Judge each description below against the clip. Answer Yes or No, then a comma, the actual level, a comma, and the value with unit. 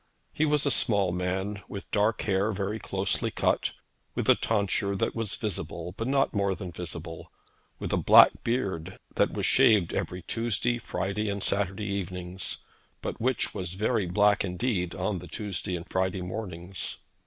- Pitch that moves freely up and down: No, average, 2.9 semitones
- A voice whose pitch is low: Yes, low, 100 Hz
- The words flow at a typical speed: Yes, average, 165 wpm